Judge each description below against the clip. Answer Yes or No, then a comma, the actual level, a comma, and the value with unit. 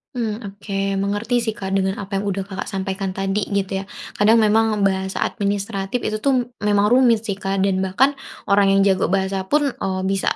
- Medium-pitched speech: No, high, 200 Hz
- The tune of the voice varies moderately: No, narrow, 2.1 semitones